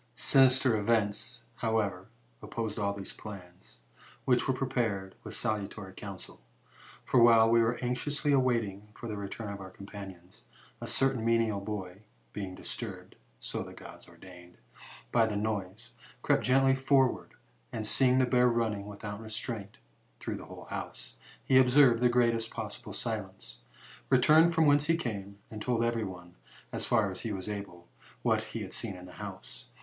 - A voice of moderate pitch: No, low, 110 Hz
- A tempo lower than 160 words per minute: No, average, 165 wpm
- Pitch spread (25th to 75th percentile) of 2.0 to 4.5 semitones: Yes, average, 3.8 semitones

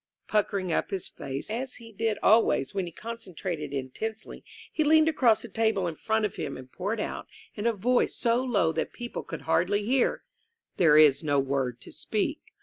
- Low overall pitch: No, high, 205 Hz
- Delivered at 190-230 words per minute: Yes, average, 195 wpm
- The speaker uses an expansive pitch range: Yes, wide, 6.3 semitones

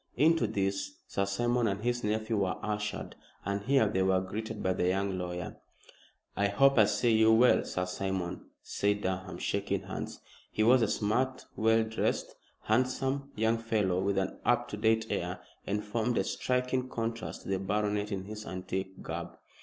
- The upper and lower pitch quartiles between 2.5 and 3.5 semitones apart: Yes, average, 2.9 semitones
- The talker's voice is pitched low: Yes, low, 105 Hz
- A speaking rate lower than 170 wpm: No, average, 175 wpm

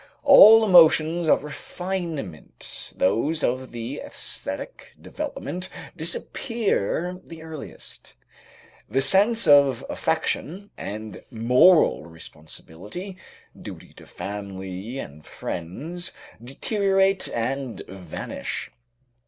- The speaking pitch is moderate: Yes, medium, 150 Hz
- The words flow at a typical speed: No, slow, 85 wpm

